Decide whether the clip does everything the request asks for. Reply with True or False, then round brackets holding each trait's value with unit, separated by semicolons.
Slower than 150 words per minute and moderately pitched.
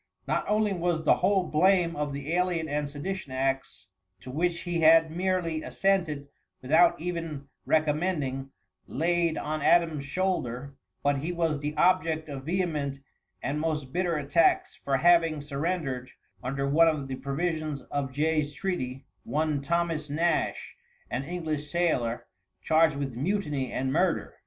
True (140 wpm; 155 Hz)